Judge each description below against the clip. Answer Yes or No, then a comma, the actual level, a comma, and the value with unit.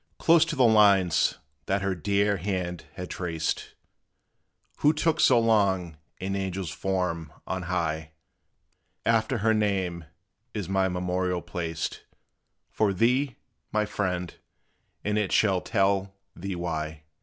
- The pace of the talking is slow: Yes, slow, 125 wpm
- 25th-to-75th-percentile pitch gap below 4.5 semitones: Yes, average, 3.0 semitones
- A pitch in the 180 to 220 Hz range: No, very low, 95 Hz